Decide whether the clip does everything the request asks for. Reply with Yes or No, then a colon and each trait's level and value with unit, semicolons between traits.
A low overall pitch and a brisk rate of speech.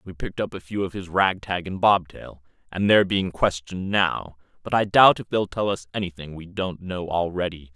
Yes: very low, 90 Hz; fast, 210 wpm